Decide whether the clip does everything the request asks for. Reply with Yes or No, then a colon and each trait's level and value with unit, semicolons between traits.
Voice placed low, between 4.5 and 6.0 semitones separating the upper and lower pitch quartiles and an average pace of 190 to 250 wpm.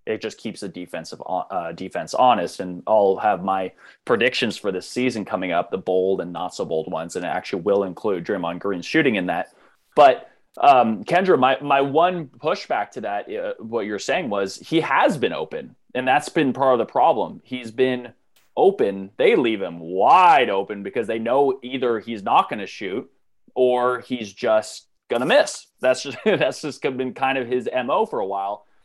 Yes: low, 125 Hz; average, 5.0 semitones; average, 195 wpm